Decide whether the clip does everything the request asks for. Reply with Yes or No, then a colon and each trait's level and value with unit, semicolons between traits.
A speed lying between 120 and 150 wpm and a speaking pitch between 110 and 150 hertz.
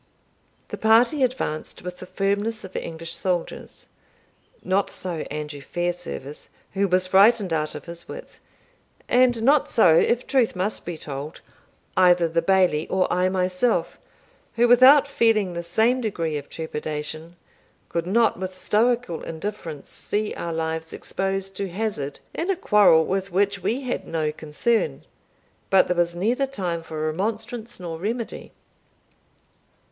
No: average, 140 wpm; medium, 185 Hz